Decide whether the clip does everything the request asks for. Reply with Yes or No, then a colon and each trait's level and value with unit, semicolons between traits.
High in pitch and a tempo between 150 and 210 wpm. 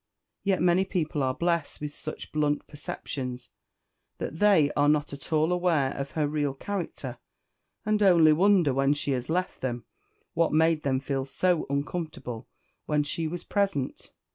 No: medium, 150 Hz; average, 160 wpm